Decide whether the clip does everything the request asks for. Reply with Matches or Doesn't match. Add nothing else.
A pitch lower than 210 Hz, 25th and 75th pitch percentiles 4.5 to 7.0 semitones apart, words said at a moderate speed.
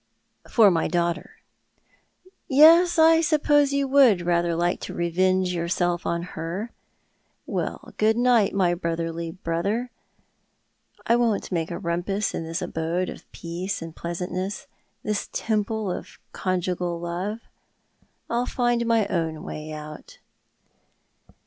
Doesn't match